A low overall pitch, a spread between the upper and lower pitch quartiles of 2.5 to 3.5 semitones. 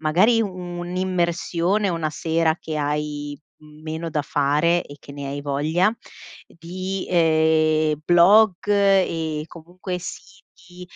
No: medium, 165 Hz; average, 2.9 semitones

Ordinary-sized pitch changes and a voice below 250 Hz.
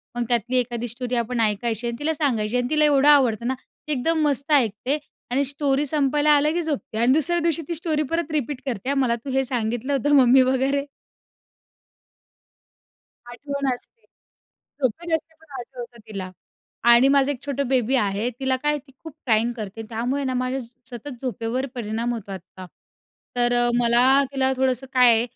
No: average, 3.1 semitones; very high, 255 Hz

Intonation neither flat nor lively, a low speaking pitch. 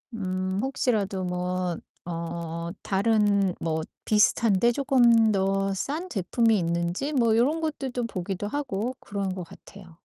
No: average, 4.5 semitones; high, 200 Hz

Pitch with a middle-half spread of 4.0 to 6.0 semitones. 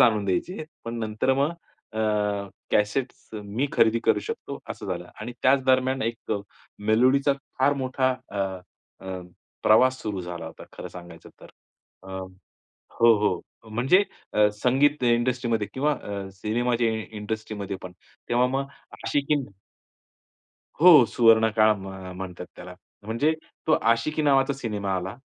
Yes: average, 4.4 semitones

